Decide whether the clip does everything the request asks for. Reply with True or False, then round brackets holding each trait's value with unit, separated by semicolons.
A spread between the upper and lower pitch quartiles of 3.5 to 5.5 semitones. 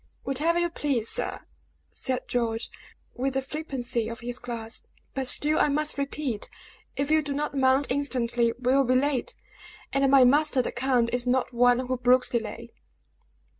False (2.5 semitones)